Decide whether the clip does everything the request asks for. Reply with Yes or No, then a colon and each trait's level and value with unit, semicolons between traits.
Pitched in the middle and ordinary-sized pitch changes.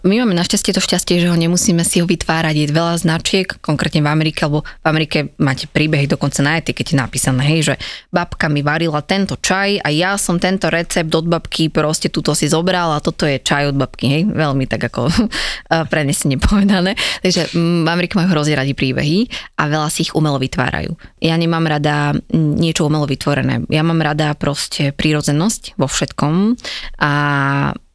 Yes: medium, 160 Hz; average, 3.1 semitones